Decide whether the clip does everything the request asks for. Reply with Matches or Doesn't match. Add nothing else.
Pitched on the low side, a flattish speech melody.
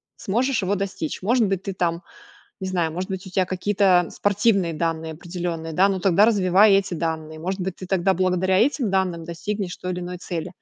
Doesn't match